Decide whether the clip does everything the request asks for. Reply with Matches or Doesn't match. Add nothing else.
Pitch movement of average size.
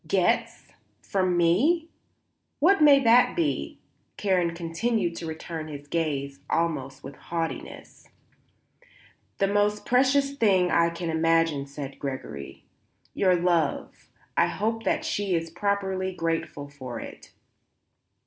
Matches